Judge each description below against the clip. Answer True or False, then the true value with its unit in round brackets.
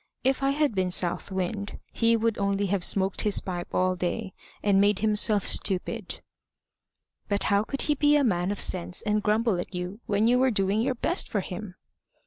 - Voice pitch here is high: True (205 Hz)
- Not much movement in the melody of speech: False (3.3 semitones)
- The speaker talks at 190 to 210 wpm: True (195 wpm)